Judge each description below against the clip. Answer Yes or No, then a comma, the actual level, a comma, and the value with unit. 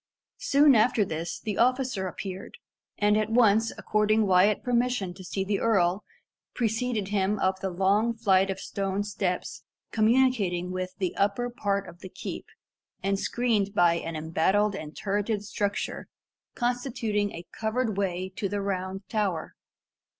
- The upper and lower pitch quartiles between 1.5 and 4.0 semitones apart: Yes, average, 2.9 semitones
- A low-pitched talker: No, high, 200 Hz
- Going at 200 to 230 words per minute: No, average, 145 wpm